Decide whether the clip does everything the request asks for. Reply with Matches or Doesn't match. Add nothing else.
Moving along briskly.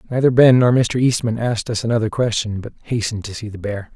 Matches